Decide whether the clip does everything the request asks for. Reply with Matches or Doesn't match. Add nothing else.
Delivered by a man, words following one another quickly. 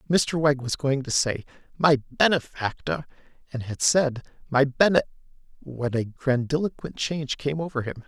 Doesn't match